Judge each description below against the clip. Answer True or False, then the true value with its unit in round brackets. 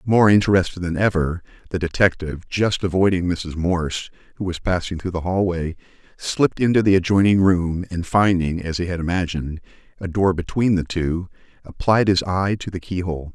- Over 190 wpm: False (170 wpm)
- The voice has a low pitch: True (90 Hz)